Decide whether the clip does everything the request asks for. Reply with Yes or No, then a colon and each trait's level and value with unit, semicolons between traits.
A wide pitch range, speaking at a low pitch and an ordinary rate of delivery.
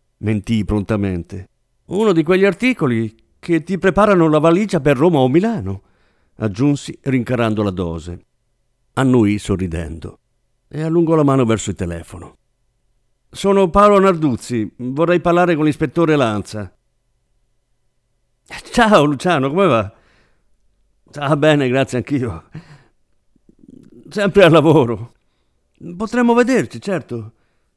No: wide, 8.0 semitones; low, 130 Hz; slow, 110 wpm